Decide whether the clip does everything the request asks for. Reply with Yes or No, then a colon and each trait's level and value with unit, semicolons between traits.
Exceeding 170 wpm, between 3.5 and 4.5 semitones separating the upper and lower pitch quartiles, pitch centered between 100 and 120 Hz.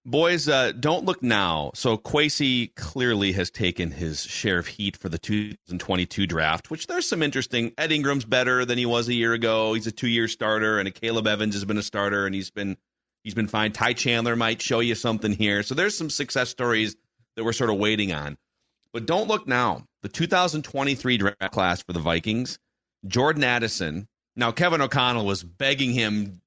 Yes: average, 195 wpm; average, 3.9 semitones; low, 115 Hz